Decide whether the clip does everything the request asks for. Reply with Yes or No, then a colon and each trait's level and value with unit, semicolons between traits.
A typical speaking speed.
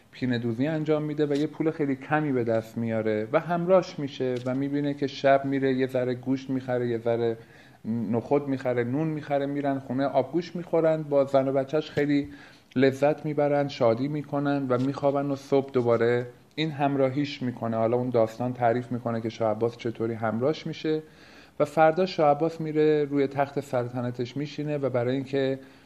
No: fast, 170 wpm